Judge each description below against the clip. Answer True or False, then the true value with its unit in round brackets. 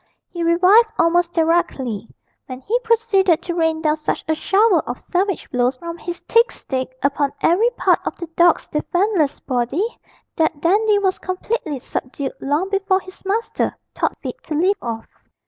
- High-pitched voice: True (340 Hz)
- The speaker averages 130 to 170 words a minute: True (165 wpm)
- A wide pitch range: False (4.9 semitones)